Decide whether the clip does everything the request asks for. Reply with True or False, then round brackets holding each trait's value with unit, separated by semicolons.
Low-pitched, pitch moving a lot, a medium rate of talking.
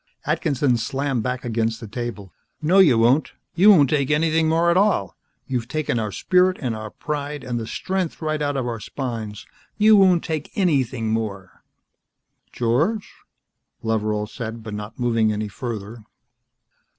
True (125 Hz; 5.7 semitones; 155 wpm)